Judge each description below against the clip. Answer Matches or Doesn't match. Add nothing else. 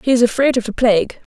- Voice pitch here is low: Doesn't match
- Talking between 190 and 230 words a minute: Doesn't match